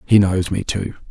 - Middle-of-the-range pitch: No, very low, 95 Hz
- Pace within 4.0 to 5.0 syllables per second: Yes, 4.7 syllables/s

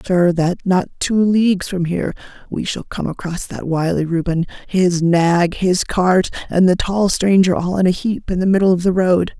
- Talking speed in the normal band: No, fast, 215 wpm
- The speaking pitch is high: No, medium, 180 Hz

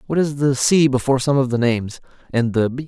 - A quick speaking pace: Yes, fast, 250 wpm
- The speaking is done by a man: Yes, male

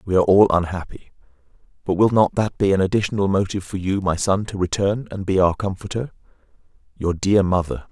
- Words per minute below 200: Yes, average, 190 wpm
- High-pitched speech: No, very low, 95 Hz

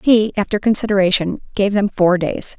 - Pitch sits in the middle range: No, high, 200 Hz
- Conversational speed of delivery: Yes, average, 160 wpm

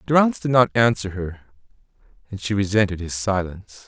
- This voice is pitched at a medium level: No, low, 105 Hz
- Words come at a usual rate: Yes, average, 155 wpm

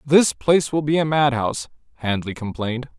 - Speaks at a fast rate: No, average, 160 wpm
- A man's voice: Yes, male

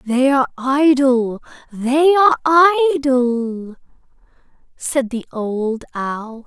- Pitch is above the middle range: Yes, very high, 265 Hz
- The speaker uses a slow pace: Yes, slow, 95 wpm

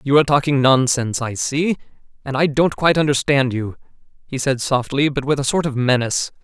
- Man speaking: Yes, male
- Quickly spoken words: No, average, 195 wpm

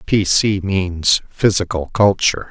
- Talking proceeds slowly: Yes, slow, 120 wpm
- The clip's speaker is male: Yes, male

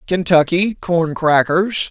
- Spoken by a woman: No, male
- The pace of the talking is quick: No, slow, 95 wpm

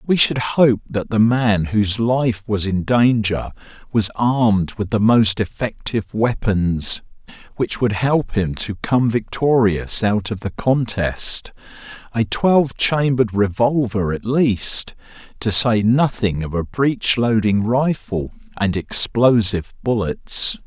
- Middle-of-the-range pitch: No, low, 110 Hz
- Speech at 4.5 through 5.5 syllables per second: No, 3.7 syllables/s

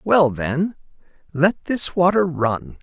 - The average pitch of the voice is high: No, medium, 160 Hz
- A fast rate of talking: No, slow, 125 wpm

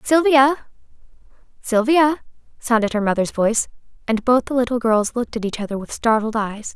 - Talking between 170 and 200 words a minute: No, average, 160 wpm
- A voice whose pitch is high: Yes, high, 240 Hz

